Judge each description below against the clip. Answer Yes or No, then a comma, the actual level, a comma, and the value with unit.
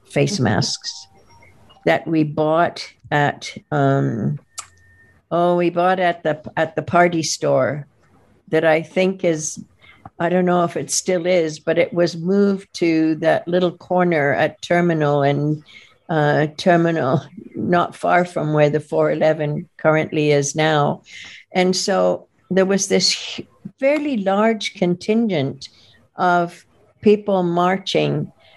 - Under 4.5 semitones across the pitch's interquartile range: Yes, average, 3.6 semitones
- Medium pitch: Yes, medium, 160 Hz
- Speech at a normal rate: No, slow, 125 wpm